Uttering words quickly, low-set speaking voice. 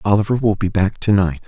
Yes: fast, 245 wpm; low, 100 Hz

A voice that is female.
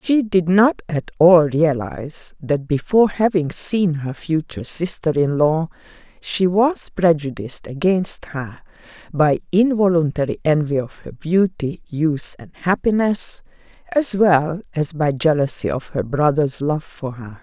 Yes: female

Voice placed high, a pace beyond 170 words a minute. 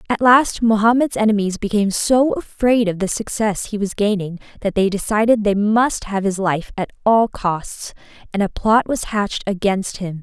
Yes: high, 210 Hz; average, 180 wpm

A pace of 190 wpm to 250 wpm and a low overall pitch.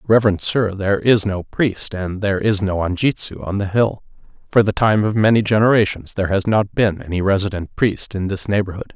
Yes: average, 200 wpm; low, 100 Hz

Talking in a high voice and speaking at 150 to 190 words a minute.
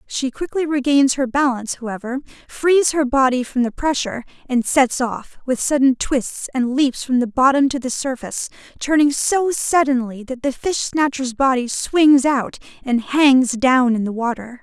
Yes: very high, 265 Hz; average, 170 wpm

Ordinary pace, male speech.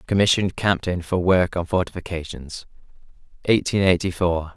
No: slow, 120 wpm; male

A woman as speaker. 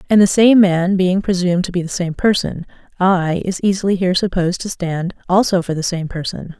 Yes: female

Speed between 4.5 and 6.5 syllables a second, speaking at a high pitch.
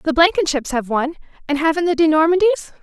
No: 7.3 syllables/s; very high, 315 Hz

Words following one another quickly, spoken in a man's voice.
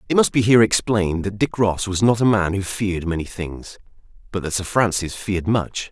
Yes: fast, 225 wpm; male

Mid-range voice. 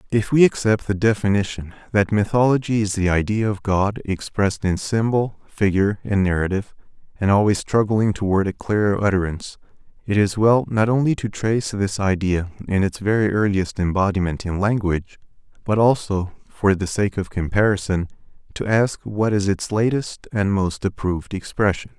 No: low, 100 Hz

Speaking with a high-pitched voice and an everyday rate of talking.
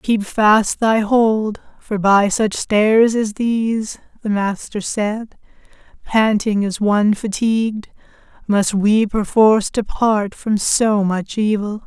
No: high, 210 Hz; slow, 125 wpm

